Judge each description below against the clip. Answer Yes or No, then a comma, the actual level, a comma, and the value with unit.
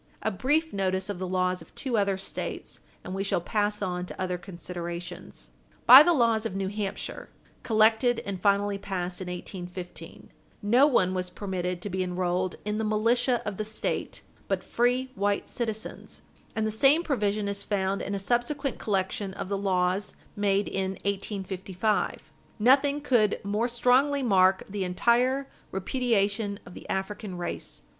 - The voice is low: No, high, 200 Hz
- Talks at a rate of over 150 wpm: Yes, average, 160 wpm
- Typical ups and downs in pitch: Yes, average, 3.6 semitones